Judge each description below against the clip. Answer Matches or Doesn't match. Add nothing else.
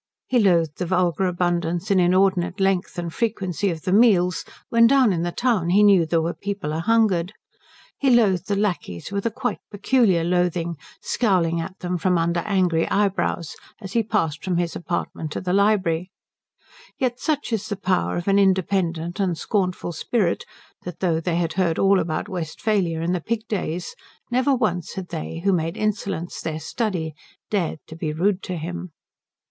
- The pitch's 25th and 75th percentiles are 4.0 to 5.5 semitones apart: Doesn't match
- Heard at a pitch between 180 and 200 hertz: Matches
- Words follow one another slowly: Doesn't match